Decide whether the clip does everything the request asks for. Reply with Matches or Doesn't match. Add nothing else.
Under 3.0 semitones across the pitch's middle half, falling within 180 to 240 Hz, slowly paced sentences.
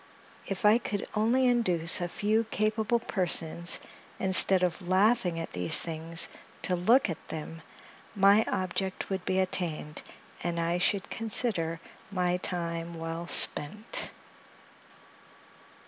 Doesn't match